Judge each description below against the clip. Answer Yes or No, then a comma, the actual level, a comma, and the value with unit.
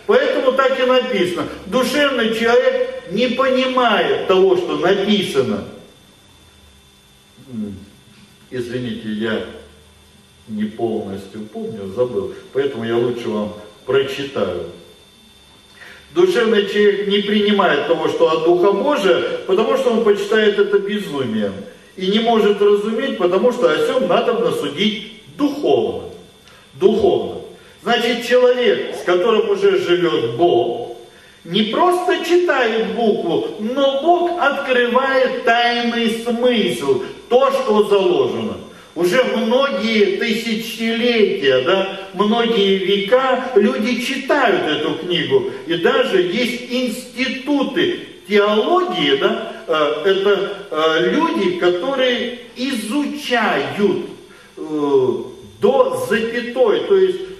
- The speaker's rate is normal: No, slow, 95 wpm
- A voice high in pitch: Yes, high, 235 Hz